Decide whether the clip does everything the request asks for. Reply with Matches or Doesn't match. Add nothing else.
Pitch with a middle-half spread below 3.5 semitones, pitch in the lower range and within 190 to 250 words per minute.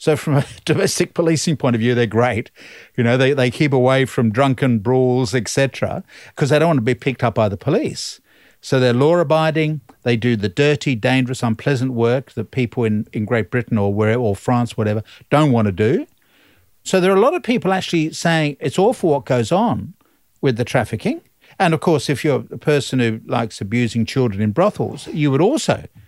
Doesn't match